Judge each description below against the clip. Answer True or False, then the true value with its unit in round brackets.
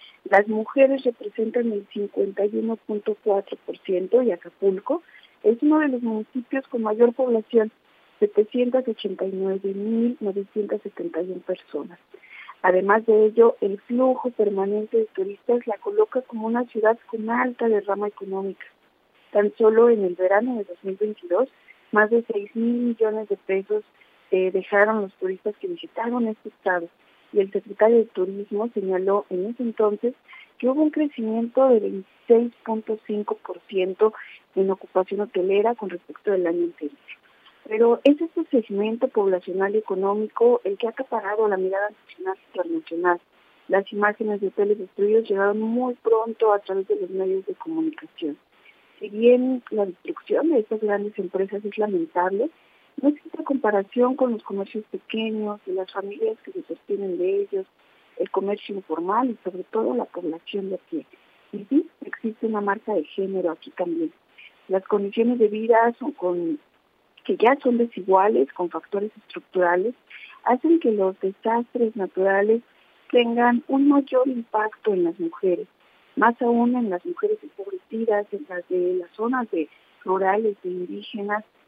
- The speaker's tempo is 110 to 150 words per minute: True (140 wpm)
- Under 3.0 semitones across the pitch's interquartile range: False (3.7 semitones)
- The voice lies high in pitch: True (215 Hz)